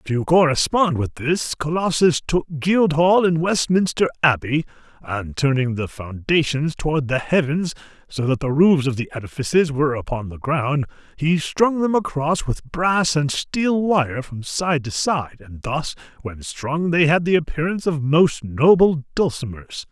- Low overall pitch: No, medium, 150 Hz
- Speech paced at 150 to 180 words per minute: Yes, average, 160 wpm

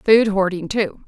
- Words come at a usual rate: Yes, average, 170 wpm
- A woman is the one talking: Yes, female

